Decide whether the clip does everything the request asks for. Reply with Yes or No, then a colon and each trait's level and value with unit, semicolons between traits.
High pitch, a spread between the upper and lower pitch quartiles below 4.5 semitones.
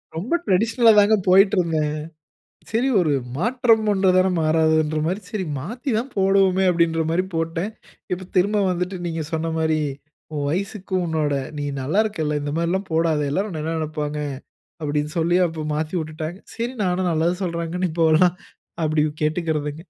No: medium, 170 Hz; average, 3.5 semitones